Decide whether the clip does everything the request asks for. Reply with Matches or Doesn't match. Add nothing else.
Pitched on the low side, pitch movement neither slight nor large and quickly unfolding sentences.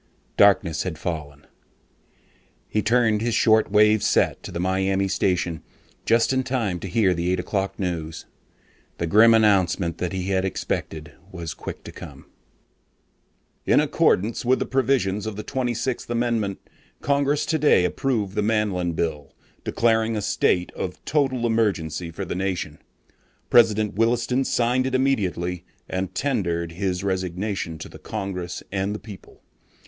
Doesn't match